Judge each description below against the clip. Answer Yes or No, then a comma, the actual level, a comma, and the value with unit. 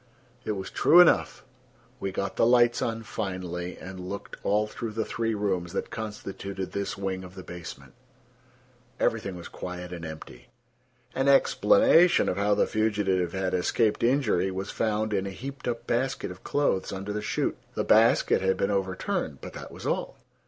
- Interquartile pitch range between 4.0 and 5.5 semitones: No, average, 3.4 semitones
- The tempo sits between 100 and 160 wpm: No, average, 175 wpm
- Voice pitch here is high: No, low, 100 Hz